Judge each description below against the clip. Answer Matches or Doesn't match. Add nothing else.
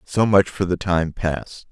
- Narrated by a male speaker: Matches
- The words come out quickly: Matches